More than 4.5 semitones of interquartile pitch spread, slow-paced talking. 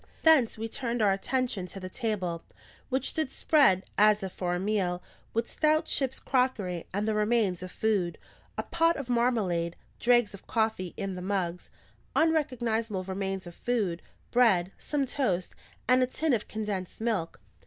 No: average, 5.2 semitones; average, 165 wpm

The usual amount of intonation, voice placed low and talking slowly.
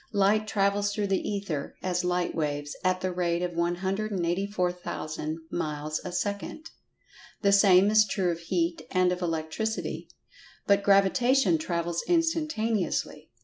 No: average, 3.0 semitones; medium, 185 Hz; slow, 130 wpm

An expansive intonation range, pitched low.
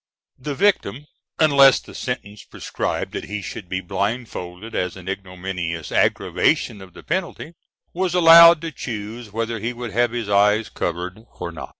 Yes: wide, 6.0 semitones; low, 110 Hz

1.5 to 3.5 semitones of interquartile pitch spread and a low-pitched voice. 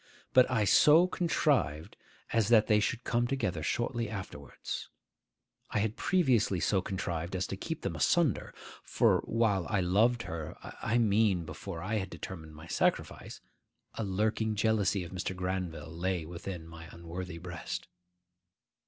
No: average, 4.7 semitones; very low, 95 Hz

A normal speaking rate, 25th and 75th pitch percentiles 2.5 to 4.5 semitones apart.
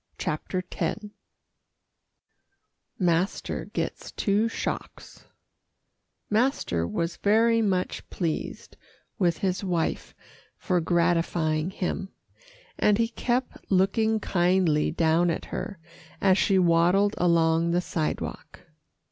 No: slow, 95 wpm; average, 3.1 semitones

